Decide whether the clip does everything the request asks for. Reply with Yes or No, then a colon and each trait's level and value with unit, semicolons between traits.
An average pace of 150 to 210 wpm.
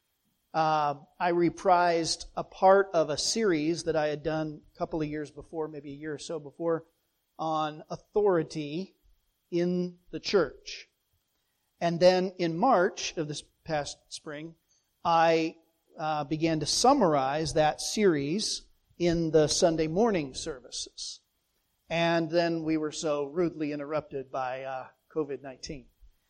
No: slow, 135 wpm